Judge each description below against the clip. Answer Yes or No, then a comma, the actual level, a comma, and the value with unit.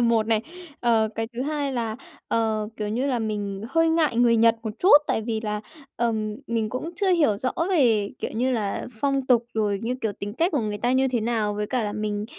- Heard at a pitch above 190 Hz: Yes, high, 230 Hz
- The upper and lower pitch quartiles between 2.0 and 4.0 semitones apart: Yes, average, 3.1 semitones